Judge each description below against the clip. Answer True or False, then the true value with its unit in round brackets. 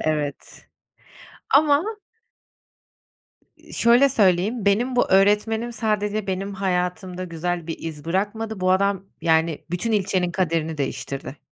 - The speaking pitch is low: False (190 Hz)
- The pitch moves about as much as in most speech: True (4.2 semitones)